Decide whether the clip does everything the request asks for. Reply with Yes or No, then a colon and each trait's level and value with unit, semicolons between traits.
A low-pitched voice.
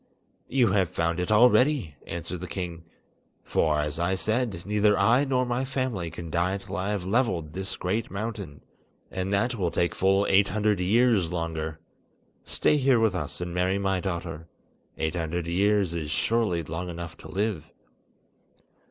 Yes: very low, 95 Hz